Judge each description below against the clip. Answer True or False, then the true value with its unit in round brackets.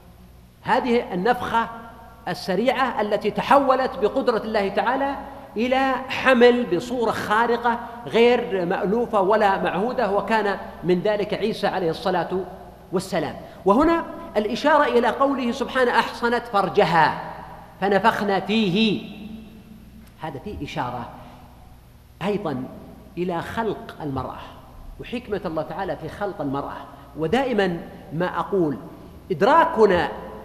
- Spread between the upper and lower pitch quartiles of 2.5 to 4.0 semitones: False (4.5 semitones)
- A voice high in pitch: True (210 Hz)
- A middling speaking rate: True (95 wpm)